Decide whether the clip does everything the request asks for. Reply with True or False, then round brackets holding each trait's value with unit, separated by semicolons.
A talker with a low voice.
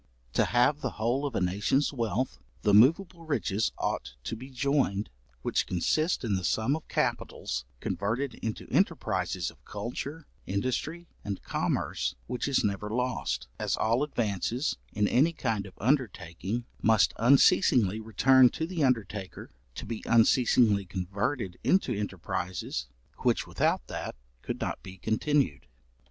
True (115 Hz)